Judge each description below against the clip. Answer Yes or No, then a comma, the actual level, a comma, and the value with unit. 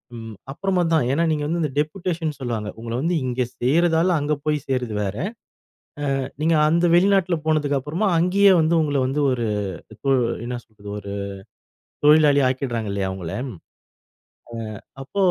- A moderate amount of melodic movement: No, wide, 5.7 semitones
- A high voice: No, medium, 145 Hz